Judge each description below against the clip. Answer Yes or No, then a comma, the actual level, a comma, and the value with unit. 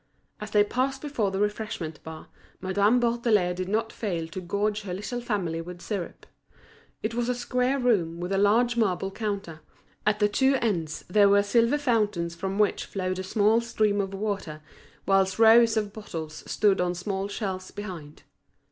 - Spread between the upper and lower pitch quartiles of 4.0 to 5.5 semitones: No, average, 3.4 semitones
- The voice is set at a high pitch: Yes, high, 205 Hz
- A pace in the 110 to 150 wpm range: No, average, 175 wpm